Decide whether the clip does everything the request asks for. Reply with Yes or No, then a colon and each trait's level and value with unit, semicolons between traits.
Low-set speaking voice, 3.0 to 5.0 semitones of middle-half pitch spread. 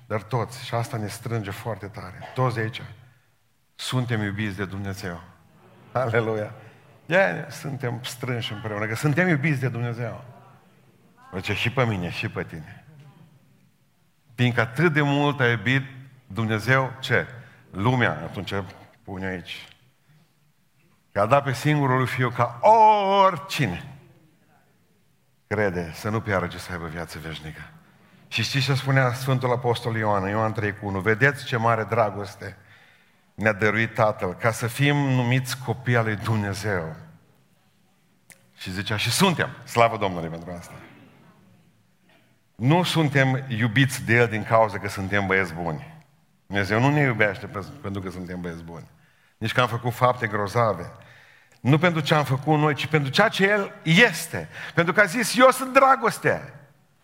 No: low, 120 Hz; wide, 5.5 semitones